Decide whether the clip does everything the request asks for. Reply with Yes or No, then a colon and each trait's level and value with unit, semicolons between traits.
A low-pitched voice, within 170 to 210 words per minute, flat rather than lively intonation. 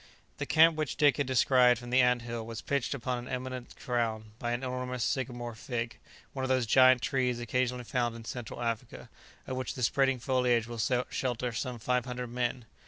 Yes: low, 125 Hz; average, 195 wpm; narrow, 1.4 semitones